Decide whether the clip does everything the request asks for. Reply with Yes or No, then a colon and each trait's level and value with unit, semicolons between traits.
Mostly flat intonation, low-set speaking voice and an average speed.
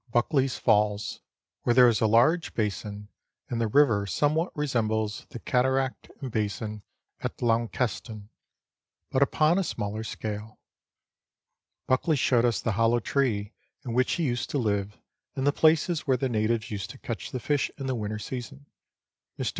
No: average, 3.9 semitones; low, 120 Hz; average, 165 wpm